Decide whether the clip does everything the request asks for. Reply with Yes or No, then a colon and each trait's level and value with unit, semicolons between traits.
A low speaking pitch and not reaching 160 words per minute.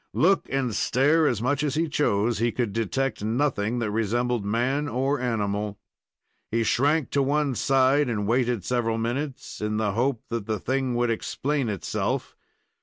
No: low, 120 Hz; average, 165 wpm